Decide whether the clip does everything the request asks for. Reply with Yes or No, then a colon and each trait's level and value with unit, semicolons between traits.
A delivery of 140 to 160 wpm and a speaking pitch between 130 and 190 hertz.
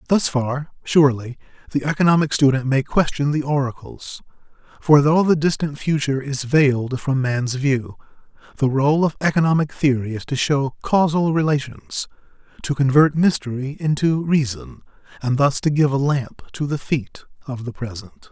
Yes: average, 155 wpm; medium, 140 Hz